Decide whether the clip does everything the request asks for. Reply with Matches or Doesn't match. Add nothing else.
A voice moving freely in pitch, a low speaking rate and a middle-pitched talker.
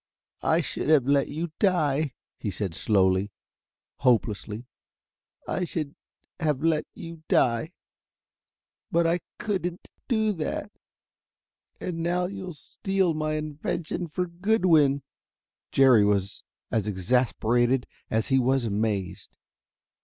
Matches